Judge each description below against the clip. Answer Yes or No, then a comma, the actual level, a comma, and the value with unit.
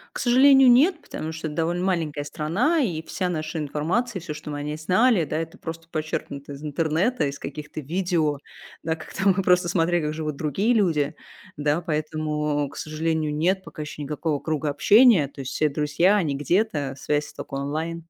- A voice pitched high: No, medium, 160 Hz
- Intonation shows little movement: No, average, 3.3 semitones